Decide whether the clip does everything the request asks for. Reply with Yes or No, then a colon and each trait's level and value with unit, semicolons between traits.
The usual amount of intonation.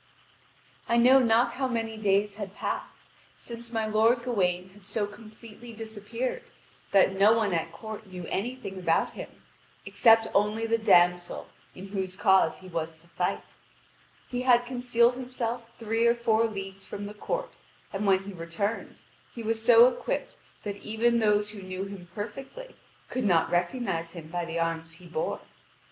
Yes: average, 3.7 semitones